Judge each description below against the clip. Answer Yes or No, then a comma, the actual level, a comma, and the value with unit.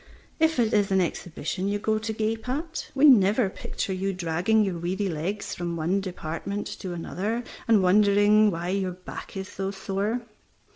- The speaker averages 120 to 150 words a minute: No, average, 175 wpm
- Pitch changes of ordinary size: Yes, average, 3.0 semitones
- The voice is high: Yes, high, 195 Hz